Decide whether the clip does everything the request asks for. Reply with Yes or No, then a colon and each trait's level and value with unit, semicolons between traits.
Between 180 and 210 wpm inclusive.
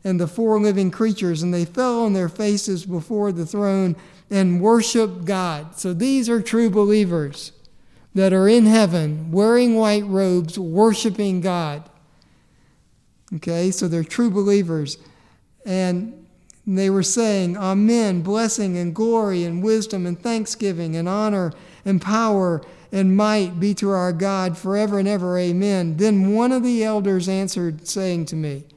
No: average, 150 wpm